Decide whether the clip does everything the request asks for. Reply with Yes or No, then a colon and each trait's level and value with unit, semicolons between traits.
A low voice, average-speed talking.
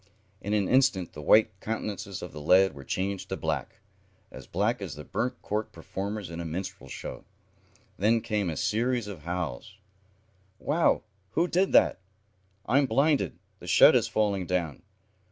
Yes: low, 100 Hz; average, 160 wpm